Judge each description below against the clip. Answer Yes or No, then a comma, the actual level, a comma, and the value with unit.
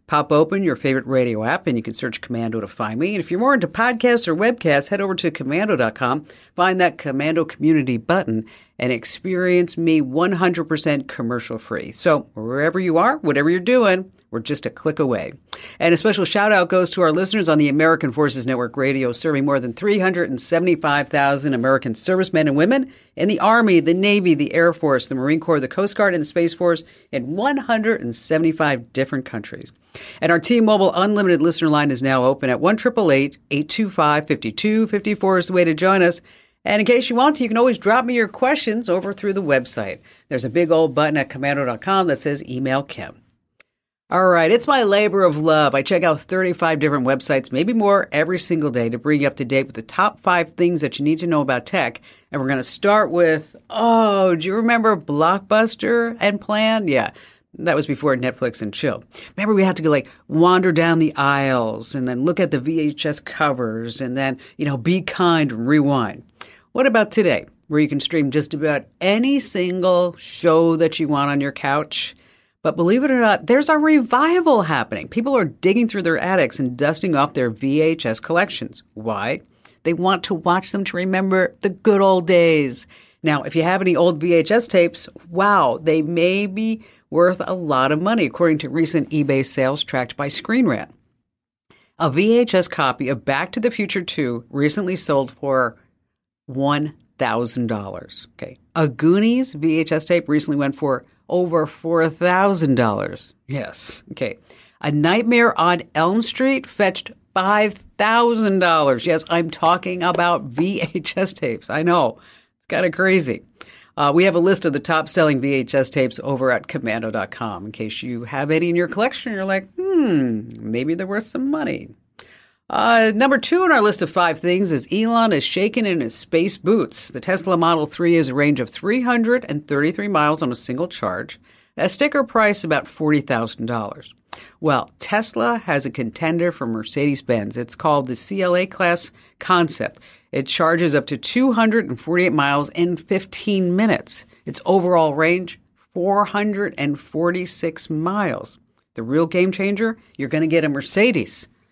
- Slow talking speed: No, average, 180 wpm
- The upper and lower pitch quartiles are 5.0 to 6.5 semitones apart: Yes, wide, 5.4 semitones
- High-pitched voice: No, medium, 165 Hz